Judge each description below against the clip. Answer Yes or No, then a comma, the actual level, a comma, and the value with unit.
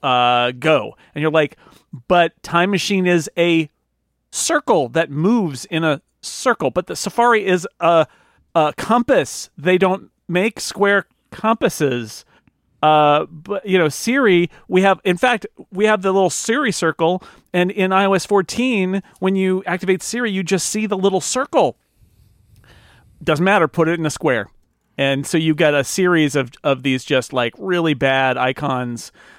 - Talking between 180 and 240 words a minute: No, average, 160 wpm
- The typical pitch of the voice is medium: Yes, medium, 170 Hz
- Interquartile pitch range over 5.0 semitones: Yes, wide, 5.5 semitones